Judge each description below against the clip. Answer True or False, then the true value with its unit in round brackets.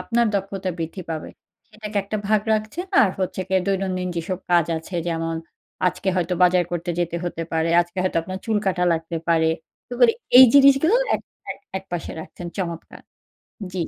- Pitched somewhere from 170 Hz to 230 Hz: True (185 Hz)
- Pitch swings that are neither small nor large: True (3.6 semitones)